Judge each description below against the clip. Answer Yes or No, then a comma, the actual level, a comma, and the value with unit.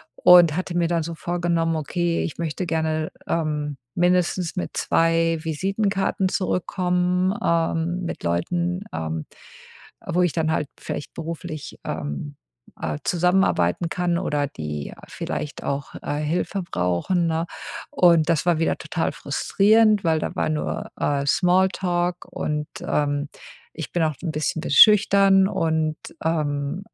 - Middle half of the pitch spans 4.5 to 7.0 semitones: No, average, 2.9 semitones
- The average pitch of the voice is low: No, medium, 165 Hz